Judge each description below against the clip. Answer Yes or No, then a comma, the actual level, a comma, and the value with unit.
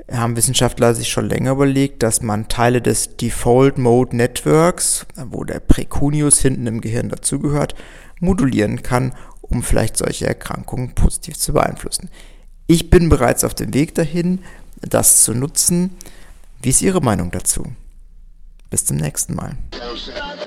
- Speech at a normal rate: Yes, average, 135 wpm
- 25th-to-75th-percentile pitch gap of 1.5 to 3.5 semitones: No, average, 3.9 semitones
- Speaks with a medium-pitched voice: No, low, 125 Hz